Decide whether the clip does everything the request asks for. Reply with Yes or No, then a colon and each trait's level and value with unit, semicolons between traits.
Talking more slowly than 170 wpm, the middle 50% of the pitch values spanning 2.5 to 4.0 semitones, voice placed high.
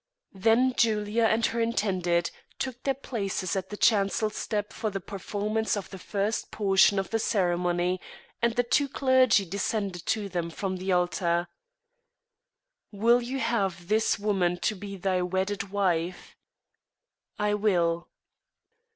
Yes: slow, 135 wpm; average, 3.2 semitones; high, 200 Hz